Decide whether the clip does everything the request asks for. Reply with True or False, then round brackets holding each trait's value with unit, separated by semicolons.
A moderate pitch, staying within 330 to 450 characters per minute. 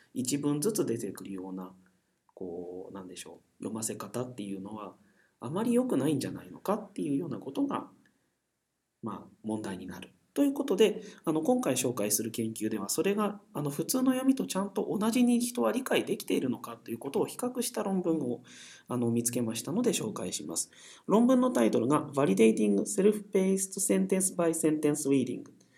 True (155 Hz; 425 characters per minute)